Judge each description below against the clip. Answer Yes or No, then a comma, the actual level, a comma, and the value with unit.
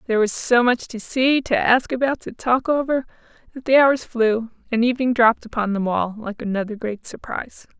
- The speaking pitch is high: Yes, high, 235 Hz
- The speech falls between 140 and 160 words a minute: No, average, 200 wpm